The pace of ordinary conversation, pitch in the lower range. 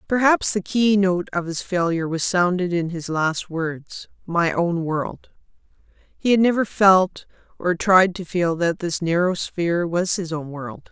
No: average, 170 wpm; medium, 180 Hz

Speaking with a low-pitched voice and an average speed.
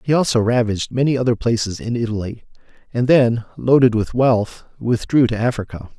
Yes: low, 120 Hz; average, 160 wpm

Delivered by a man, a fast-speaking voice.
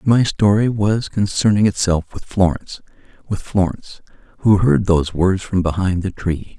No: male; average, 155 wpm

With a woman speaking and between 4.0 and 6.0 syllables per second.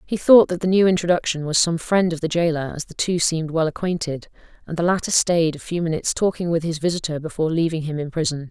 No: female; 6.4 syllables/s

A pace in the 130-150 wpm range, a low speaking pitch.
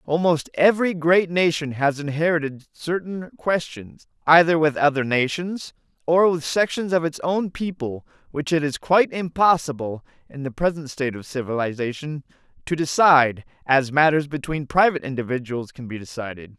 No: average, 145 wpm; medium, 150 Hz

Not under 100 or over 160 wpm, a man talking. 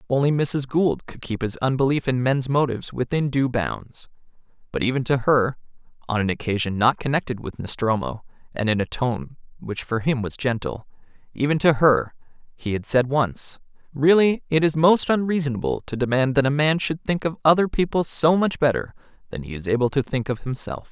No: average, 190 wpm; male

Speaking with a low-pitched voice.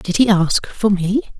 No: high, 200 Hz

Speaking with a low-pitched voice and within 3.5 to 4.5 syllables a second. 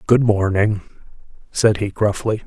Yes: low, 105 Hz; 3.9 syllables/s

